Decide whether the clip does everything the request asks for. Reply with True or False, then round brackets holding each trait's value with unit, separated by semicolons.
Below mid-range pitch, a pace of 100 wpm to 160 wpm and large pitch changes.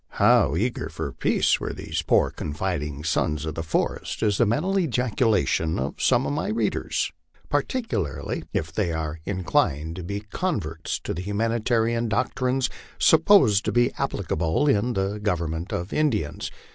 True (100 Hz; 150 wpm; 7.1 semitones)